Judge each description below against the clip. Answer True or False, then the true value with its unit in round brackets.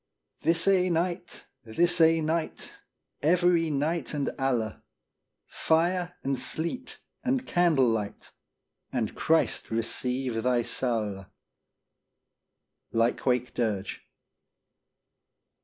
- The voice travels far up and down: True (6.2 semitones)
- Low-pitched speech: False (150 Hz)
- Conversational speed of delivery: False (90 wpm)